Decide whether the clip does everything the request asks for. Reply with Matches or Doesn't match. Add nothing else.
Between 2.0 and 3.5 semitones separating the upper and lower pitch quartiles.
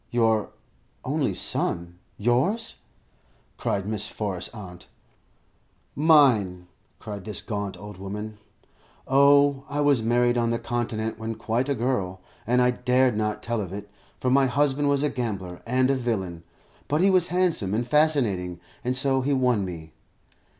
Doesn't match